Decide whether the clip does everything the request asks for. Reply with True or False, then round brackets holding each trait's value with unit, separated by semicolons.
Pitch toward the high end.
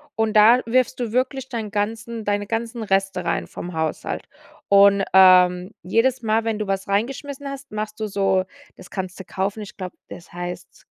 True (210 Hz)